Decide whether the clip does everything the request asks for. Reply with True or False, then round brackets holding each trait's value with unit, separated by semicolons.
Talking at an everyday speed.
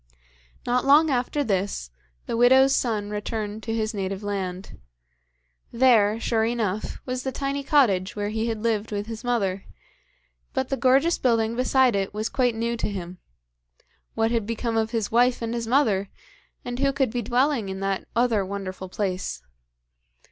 True (165 wpm)